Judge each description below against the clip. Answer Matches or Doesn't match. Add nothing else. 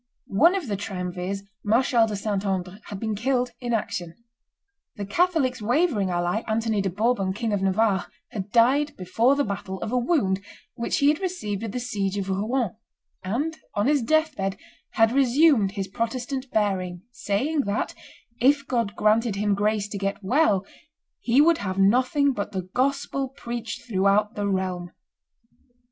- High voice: Matches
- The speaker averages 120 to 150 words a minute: Doesn't match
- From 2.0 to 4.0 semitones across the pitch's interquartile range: Doesn't match